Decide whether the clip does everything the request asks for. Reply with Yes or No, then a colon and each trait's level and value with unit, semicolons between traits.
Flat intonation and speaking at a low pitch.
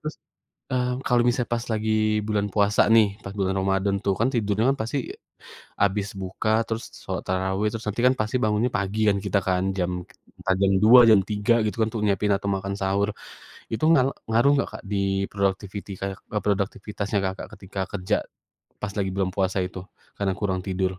Yes: narrow, 2.2 semitones; low, 100 Hz